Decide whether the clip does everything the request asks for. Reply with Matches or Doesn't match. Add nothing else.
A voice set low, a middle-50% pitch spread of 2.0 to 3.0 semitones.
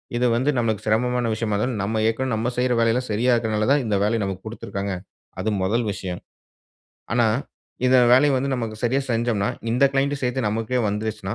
Matches